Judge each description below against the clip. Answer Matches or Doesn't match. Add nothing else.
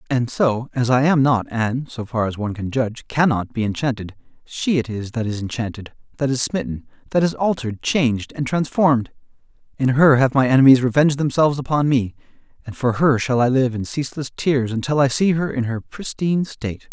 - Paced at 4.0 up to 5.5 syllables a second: Doesn't match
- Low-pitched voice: Matches